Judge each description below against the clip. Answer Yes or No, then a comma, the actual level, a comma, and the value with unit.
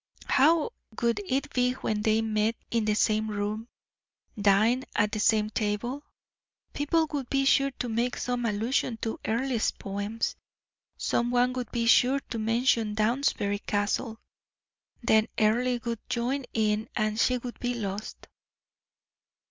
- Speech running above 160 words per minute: No, average, 140 wpm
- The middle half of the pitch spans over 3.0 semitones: No, average, 2.7 semitones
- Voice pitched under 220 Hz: No, high, 230 Hz